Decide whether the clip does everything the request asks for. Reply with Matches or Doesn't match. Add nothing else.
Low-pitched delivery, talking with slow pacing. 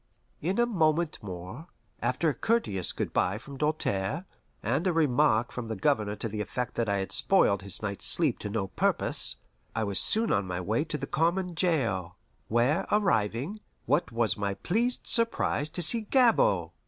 Doesn't match